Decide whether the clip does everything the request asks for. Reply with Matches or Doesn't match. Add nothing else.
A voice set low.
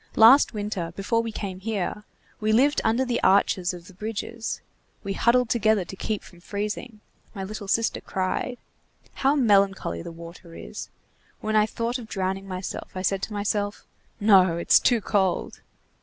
Doesn't match